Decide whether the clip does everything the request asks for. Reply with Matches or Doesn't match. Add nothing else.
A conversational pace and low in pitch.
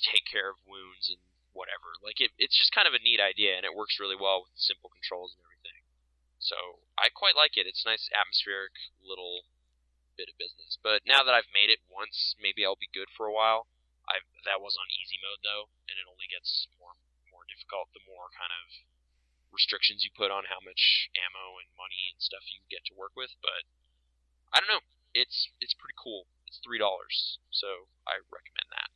Doesn't match